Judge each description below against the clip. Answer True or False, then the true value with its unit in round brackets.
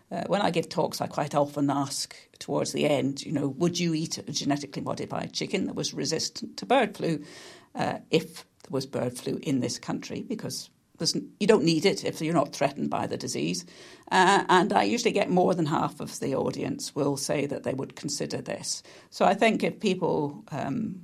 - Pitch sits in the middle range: True (160 Hz)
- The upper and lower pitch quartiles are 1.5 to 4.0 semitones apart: False (4.5 semitones)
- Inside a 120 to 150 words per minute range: False (205 wpm)